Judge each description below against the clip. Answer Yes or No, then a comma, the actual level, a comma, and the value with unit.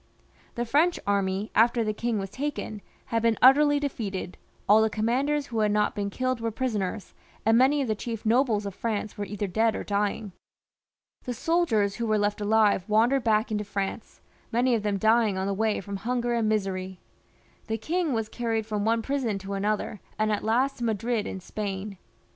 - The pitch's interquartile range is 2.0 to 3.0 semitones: Yes, average, 2.7 semitones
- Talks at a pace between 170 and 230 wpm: Yes, average, 195 wpm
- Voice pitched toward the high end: Yes, high, 220 Hz